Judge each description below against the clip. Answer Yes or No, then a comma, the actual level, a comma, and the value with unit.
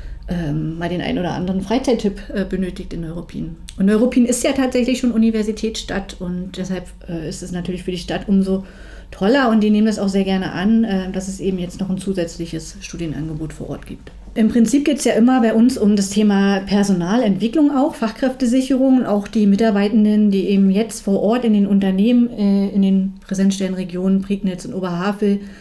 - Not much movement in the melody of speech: No, average, 3.1 semitones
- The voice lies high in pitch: Yes, high, 200 Hz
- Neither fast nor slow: Yes, average, 180 wpm